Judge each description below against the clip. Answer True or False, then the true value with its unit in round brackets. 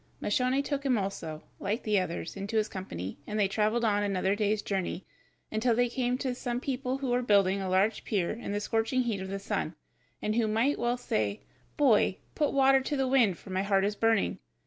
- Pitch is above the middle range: True (215 Hz)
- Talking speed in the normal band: False (215 wpm)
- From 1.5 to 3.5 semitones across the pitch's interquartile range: False (4.1 semitones)